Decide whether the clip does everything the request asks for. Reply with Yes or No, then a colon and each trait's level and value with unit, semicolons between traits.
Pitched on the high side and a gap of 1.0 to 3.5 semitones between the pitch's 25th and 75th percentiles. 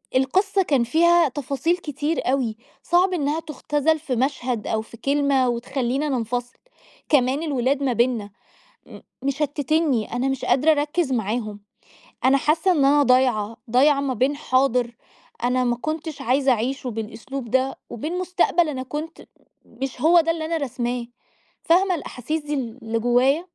No: very high, 270 Hz; average, 3.9 semitones